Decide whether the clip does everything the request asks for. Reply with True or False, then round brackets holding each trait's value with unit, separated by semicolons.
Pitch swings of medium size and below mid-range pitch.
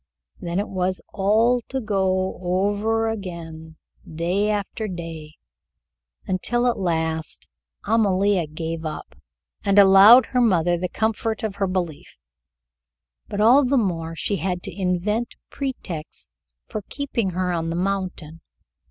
False (4.1 semitones; 190 Hz)